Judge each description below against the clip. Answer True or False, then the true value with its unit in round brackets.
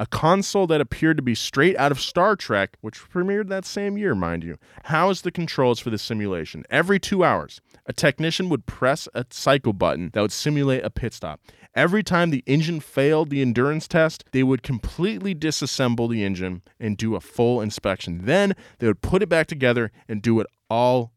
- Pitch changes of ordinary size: False (6.7 semitones)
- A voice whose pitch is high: False (135 Hz)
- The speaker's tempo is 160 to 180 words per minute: False (200 wpm)